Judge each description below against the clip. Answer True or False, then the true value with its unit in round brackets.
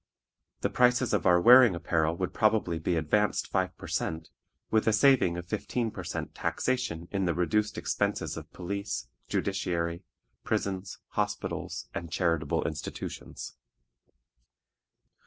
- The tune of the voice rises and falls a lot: False (4.2 semitones)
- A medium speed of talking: False (130 wpm)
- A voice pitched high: False (90 Hz)